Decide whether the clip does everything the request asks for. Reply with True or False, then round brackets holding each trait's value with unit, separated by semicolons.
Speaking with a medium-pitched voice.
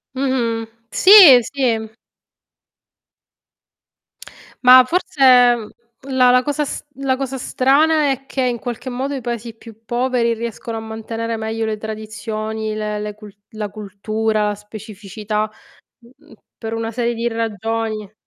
False (230 Hz)